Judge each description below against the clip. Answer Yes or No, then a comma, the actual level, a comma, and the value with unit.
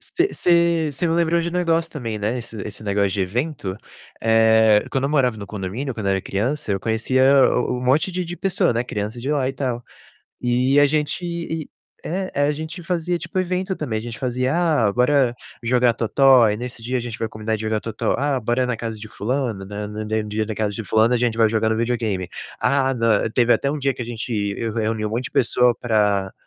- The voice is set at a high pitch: No, low, 120 Hz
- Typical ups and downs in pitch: Yes, average, 4.5 semitones